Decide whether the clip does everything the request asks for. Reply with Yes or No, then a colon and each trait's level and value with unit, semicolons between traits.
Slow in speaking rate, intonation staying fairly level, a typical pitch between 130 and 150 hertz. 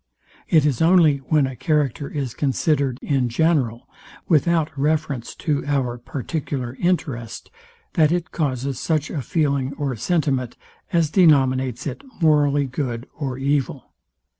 No: slow, 130 wpm; average, 3.2 semitones; medium, 140 Hz